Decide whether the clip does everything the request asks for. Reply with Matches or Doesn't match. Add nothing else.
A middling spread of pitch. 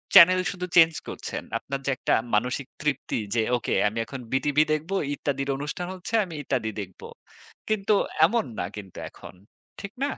Doesn't match